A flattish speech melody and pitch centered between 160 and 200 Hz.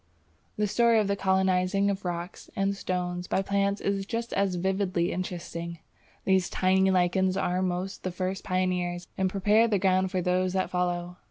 Yes: narrow, 1.5 semitones; medium, 185 Hz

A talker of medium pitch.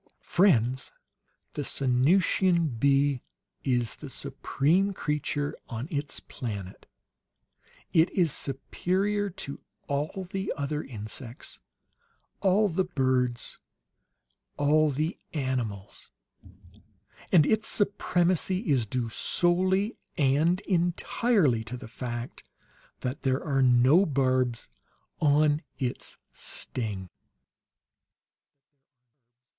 Yes: medium, 145 Hz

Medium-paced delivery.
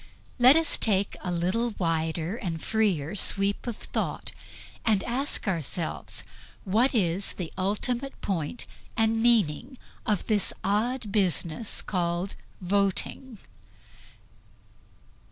No: slow, 105 wpm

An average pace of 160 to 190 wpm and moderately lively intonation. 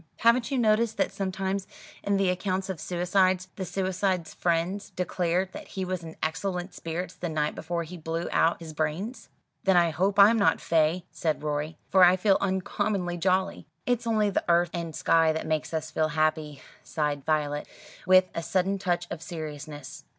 Yes: average, 180 wpm; average, 3.2 semitones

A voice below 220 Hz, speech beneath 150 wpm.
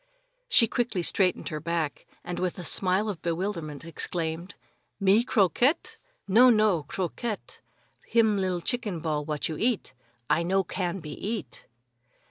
Yes: medium, 185 Hz; average, 140 wpm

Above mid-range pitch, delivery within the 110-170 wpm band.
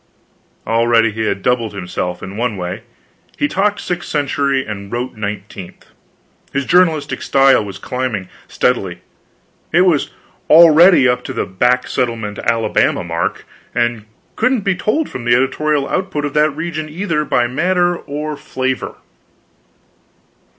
No: low, 130 Hz; slow, 135 wpm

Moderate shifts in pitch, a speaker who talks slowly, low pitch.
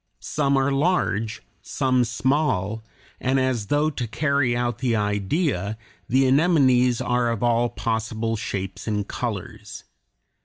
Yes: average, 3.5 semitones; slow, 125 wpm; low, 120 Hz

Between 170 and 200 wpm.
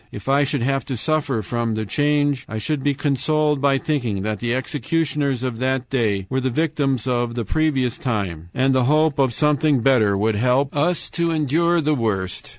Yes: average, 195 wpm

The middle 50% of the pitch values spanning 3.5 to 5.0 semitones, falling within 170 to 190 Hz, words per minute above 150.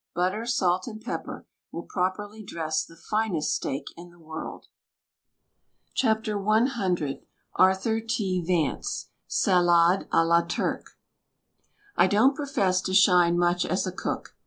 No: average, 3.9 semitones; medium, 185 Hz; average, 140 wpm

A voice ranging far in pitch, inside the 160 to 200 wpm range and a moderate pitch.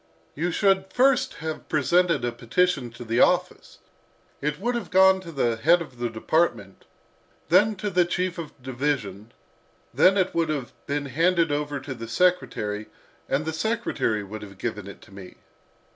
Yes: wide, 7.3 semitones; average, 175 wpm; medium, 150 Hz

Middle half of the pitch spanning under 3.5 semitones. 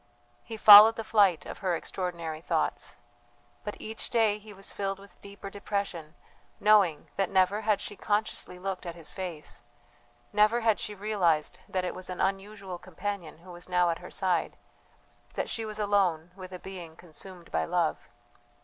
Yes: average, 2.7 semitones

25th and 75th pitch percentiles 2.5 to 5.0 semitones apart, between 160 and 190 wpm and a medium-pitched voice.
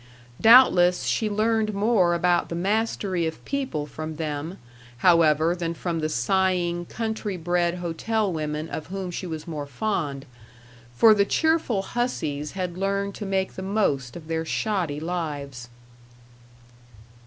No: average, 4.2 semitones; average, 140 wpm; medium, 175 Hz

